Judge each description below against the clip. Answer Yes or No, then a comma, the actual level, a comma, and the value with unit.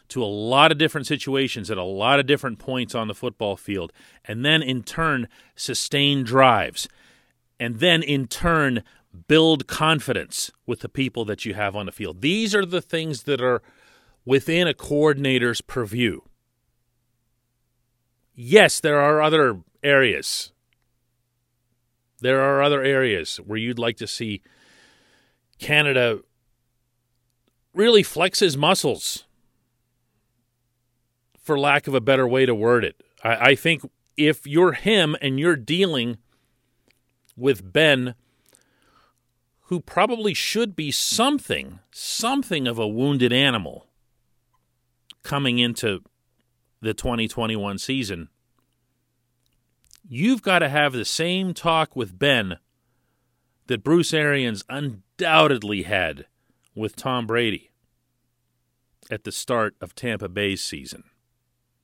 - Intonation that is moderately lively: Yes, average, 3.3 semitones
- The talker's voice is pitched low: Yes, low, 125 Hz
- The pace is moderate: No, slow, 120 wpm